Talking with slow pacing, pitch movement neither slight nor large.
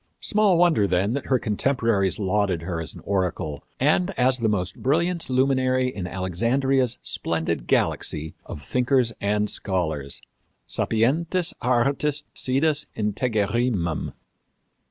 No: slow, 115 wpm; wide, 6.2 semitones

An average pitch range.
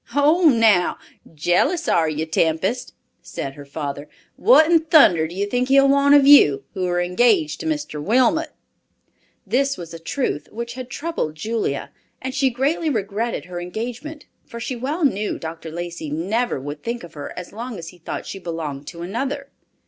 No: wide, 8.7 semitones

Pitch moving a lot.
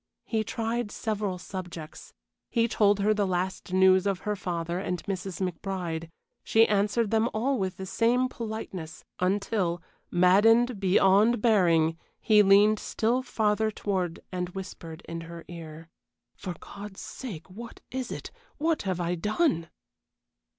No: average, 3.6 semitones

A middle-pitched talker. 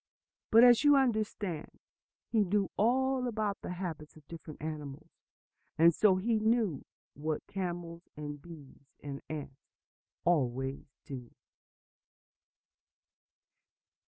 Yes: medium, 170 Hz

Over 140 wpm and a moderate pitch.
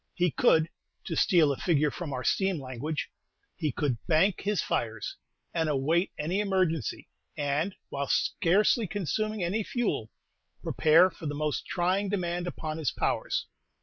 Yes: average, 150 wpm; medium, 165 Hz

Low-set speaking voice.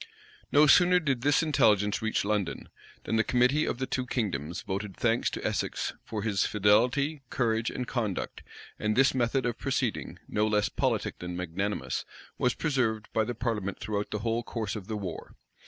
Yes: low, 110 Hz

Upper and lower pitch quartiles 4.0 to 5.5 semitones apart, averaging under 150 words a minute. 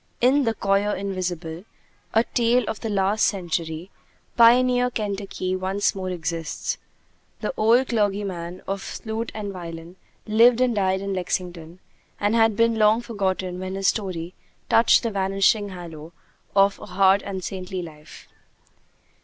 No: average, 3.3 semitones; average, 140 wpm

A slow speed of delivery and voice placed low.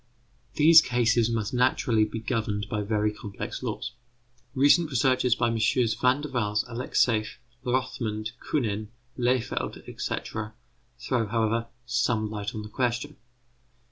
Yes: slow, 125 wpm; low, 115 Hz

